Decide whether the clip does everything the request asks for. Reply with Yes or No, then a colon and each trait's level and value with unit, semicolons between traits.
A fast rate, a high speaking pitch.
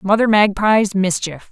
No: slow, 120 wpm; high, 200 Hz